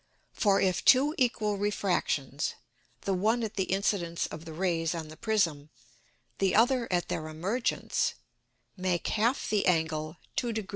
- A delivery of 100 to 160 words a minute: Yes, average, 150 wpm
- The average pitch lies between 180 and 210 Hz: Yes, high, 190 Hz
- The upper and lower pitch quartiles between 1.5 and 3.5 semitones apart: No, average, 4.8 semitones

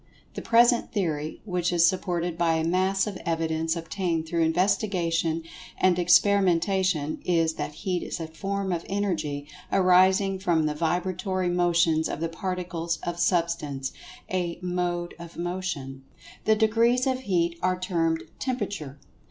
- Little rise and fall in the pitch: Yes, narrow, 2.3 semitones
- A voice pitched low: No, medium, 175 Hz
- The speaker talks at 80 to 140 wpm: Yes, slow, 135 wpm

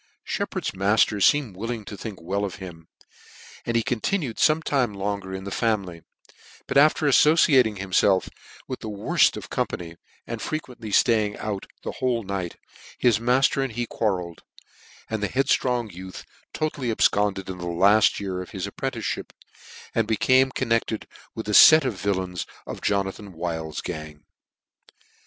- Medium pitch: No, low, 105 Hz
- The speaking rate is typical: Yes, average, 150 wpm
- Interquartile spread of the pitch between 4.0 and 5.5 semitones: Yes, average, 4.4 semitones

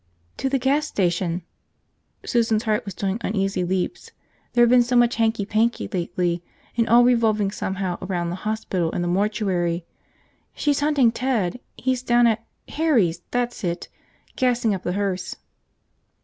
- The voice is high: Yes, high, 215 Hz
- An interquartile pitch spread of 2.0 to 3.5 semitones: No, average, 4.8 semitones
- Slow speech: No, average, 160 wpm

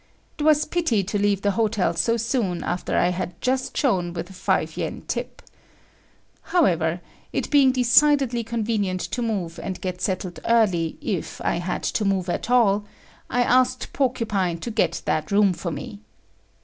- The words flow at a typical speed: Yes, average, 165 wpm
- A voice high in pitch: Yes, high, 205 Hz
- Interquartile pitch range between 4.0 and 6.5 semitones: Yes, average, 5.1 semitones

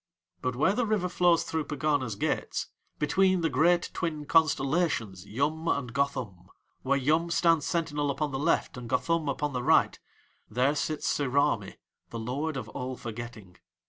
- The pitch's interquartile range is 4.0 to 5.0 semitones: Yes, average, 4.5 semitones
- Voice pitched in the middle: Yes, medium, 145 Hz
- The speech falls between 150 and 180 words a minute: Yes, average, 155 wpm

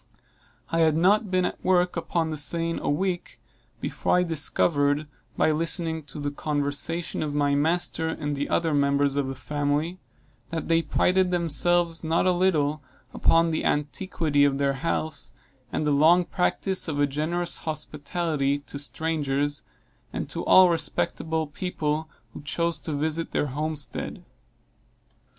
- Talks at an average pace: Yes, average, 150 wpm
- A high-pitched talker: No, medium, 155 Hz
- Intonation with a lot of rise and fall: No, average, 2.8 semitones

